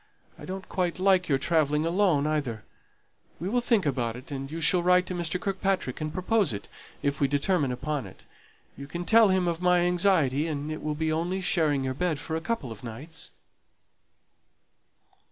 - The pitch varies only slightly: No, average, 4.3 semitones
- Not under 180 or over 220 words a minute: Yes, average, 190 wpm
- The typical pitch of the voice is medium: Yes, medium, 160 Hz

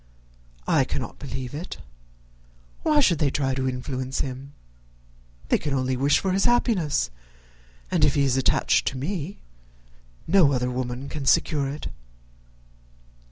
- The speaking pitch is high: No, medium, 140 Hz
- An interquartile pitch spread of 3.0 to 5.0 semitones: Yes, average, 3.4 semitones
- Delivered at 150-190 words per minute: No, slow, 135 wpm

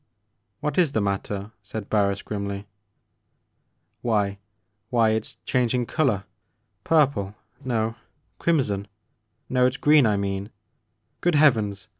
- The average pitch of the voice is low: Yes, low, 110 Hz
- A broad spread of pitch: No, average, 4.1 semitones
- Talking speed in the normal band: Yes, average, 155 wpm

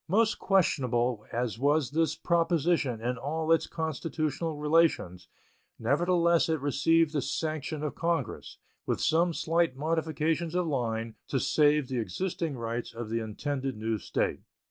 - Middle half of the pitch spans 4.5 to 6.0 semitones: Yes, average, 4.9 semitones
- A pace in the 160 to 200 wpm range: No, average, 140 wpm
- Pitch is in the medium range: Yes, medium, 150 Hz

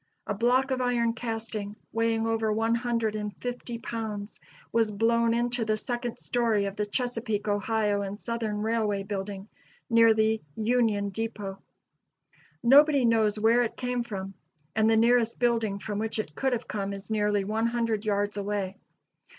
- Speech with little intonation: Yes, narrow, 2.2 semitones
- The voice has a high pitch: Yes, high, 225 Hz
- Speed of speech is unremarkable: Yes, average, 160 wpm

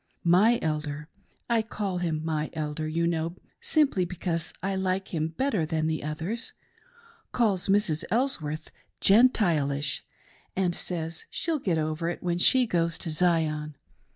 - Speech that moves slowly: No, average, 150 wpm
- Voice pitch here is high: No, medium, 170 Hz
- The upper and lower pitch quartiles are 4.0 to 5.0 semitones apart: Yes, average, 4.3 semitones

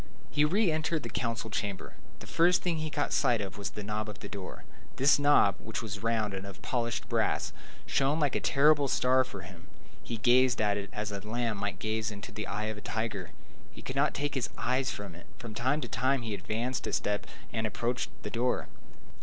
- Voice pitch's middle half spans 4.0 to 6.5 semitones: Yes, average, 4.3 semitones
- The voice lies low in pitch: Yes, low, 115 Hz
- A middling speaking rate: No, fast, 220 wpm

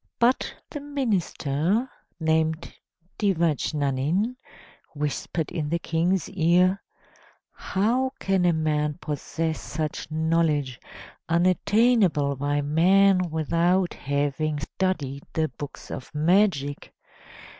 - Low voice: No, medium, 165 Hz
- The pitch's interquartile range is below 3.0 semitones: No, average, 4.2 semitones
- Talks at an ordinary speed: No, slow, 90 wpm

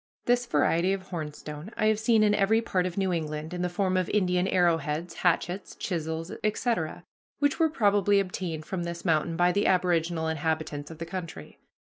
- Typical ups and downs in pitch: Yes, average, 3.5 semitones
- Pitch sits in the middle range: Yes, medium, 180 Hz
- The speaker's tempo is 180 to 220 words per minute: Yes, average, 185 wpm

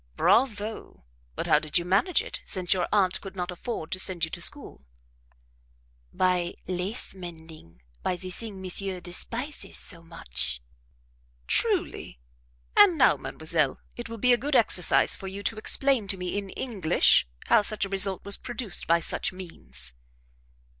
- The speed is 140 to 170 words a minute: Yes, average, 160 wpm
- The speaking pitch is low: No, high, 190 Hz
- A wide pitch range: No, average, 3.9 semitones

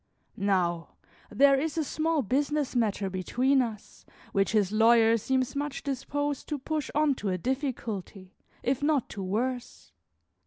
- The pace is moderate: Yes, average, 145 wpm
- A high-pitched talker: Yes, very high, 255 Hz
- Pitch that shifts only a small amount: No, average, 5.3 semitones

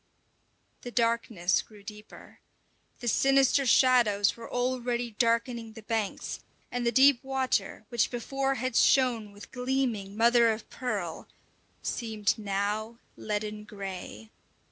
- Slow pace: Yes, slow, 120 wpm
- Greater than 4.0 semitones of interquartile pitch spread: No, average, 2.9 semitones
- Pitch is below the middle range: No, high, 230 Hz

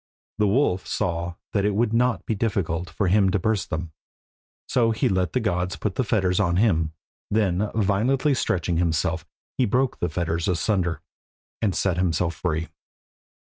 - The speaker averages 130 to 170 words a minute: Yes, average, 165 wpm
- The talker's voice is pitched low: Yes, very low, 95 Hz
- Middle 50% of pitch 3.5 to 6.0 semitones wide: Yes, average, 3.8 semitones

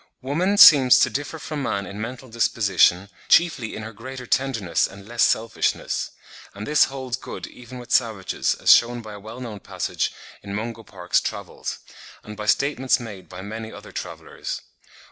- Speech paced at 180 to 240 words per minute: No, average, 170 wpm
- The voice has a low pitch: Yes, low, 115 Hz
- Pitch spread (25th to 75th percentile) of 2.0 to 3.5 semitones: No, average, 4.0 semitones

